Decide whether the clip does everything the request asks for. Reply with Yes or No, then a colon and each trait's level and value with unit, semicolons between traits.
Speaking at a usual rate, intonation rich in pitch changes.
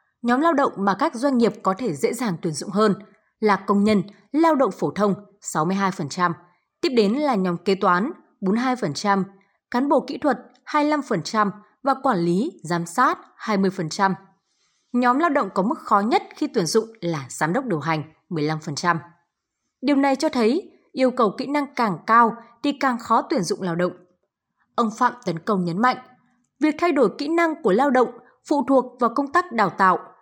Yes: average, 185 wpm; wide, 6.3 semitones